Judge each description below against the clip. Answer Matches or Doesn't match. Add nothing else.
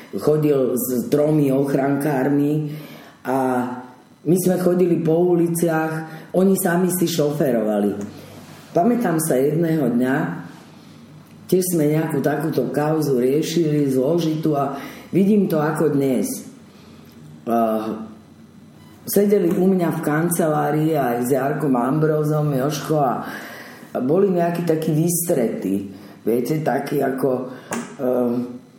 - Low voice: Doesn't match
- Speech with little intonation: Doesn't match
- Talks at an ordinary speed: Doesn't match